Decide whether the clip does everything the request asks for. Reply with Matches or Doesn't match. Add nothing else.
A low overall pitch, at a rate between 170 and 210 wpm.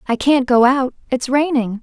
Doesn't match